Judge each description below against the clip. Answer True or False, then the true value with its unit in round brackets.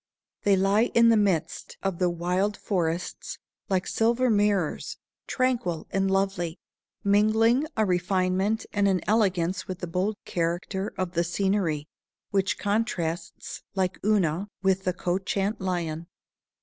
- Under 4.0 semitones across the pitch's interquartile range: True (2.6 semitones)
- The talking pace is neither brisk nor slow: False (130 wpm)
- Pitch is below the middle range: False (190 Hz)